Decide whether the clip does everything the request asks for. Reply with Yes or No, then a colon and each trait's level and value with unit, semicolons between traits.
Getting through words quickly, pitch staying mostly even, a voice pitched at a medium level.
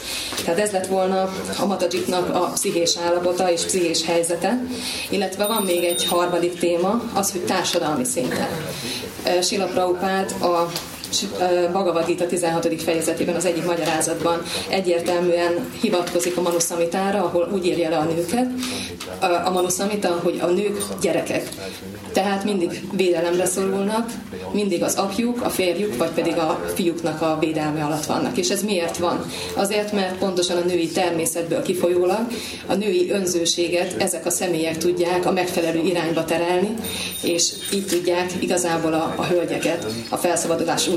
No: average, 140 wpm; narrow, 2.1 semitones; medium, 175 Hz